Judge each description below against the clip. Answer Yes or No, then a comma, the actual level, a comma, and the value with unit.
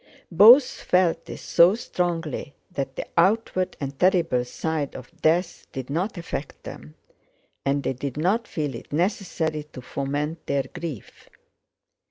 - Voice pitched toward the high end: No, medium, 160 Hz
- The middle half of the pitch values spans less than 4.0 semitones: No, average, 4.4 semitones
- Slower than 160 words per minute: Yes, average, 140 wpm